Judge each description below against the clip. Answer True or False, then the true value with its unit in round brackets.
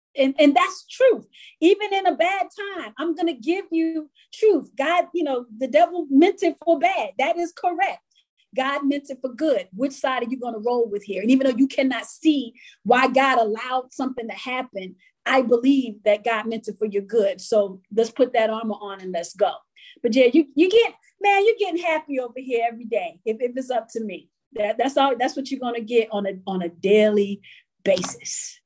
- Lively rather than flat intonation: True (6.7 semitones)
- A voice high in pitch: True (265 Hz)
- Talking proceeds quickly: True (215 wpm)